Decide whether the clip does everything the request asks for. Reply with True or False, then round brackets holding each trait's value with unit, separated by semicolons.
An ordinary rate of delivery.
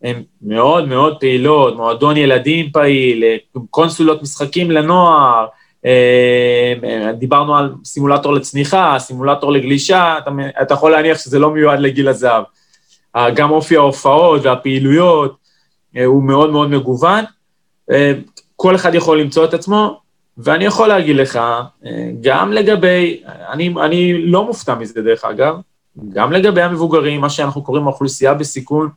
True (125 wpm)